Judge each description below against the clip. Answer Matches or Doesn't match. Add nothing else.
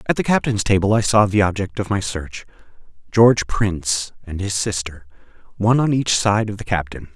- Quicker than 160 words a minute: Matches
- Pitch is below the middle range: Matches